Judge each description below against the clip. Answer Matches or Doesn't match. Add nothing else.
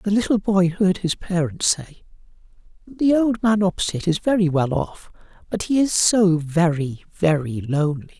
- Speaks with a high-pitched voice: Doesn't match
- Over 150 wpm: Matches